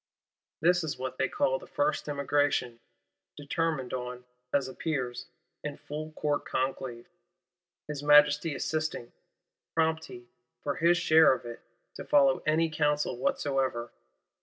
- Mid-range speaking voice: Yes, medium, 145 Hz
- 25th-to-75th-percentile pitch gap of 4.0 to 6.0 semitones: No, average, 3.1 semitones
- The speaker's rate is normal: No, slow, 130 wpm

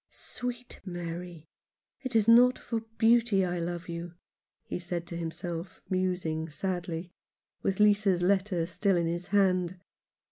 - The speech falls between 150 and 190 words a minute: No, average, 140 wpm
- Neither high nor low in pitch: Yes, medium, 180 Hz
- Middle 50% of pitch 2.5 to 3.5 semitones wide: Yes, average, 2.9 semitones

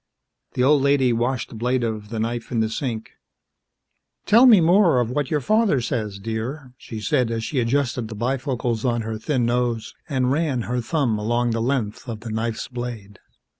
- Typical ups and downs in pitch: Yes, average, 3.0 semitones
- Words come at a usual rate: Yes, average, 190 wpm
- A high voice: No, low, 120 Hz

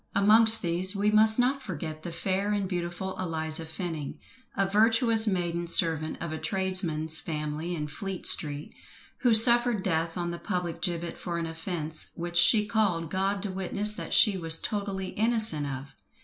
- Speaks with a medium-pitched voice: Yes, medium, 180 Hz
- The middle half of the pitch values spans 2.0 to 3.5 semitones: No, average, 4.1 semitones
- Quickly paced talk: No, average, 165 wpm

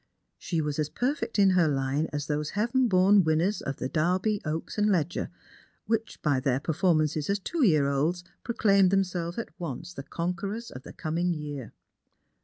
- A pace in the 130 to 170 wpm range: No, average, 180 wpm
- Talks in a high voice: No, medium, 170 Hz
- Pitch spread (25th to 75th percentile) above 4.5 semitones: Yes, average, 4.9 semitones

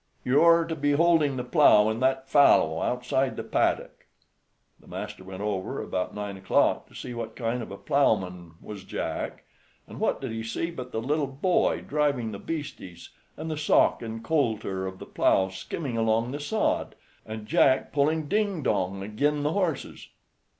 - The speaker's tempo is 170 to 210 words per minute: Yes, average, 180 wpm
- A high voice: No, low, 125 Hz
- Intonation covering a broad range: Yes, wide, 5.8 semitones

